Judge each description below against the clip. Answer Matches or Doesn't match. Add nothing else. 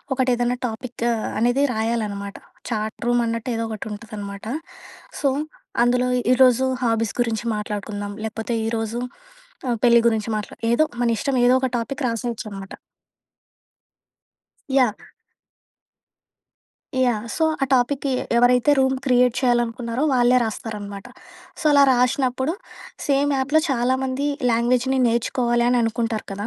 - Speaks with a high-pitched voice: Matches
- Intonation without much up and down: Matches